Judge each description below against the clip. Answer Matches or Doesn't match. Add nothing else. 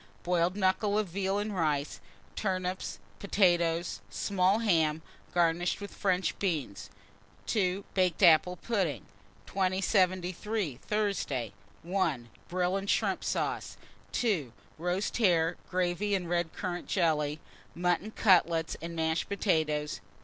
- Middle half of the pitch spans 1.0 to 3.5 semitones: Matches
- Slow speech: Matches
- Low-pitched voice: Doesn't match